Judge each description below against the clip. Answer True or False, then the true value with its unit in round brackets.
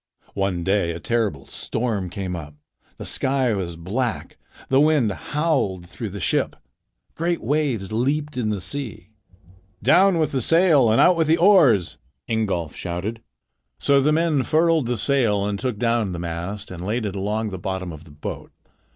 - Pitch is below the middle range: True (110 Hz)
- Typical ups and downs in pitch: False (6.9 semitones)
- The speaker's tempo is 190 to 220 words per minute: False (170 wpm)